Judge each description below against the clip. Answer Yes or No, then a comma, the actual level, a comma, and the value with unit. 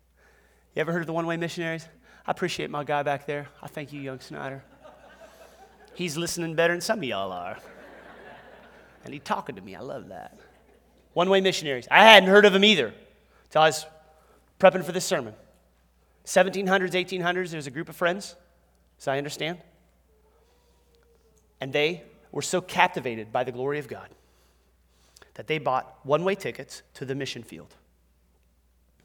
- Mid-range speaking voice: Yes, medium, 155 Hz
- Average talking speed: Yes, average, 170 wpm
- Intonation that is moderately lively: No, wide, 5.9 semitones